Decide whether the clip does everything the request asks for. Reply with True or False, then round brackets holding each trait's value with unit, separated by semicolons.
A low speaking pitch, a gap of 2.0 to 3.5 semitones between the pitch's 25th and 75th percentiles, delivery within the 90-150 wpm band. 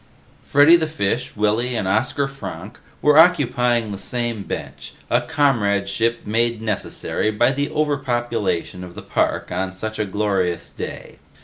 False (115 Hz; 5.0 semitones; 140 wpm)